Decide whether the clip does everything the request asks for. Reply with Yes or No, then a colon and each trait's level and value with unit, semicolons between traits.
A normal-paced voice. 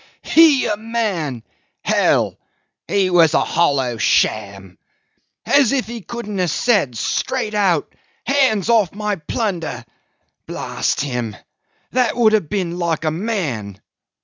No: slow, 125 wpm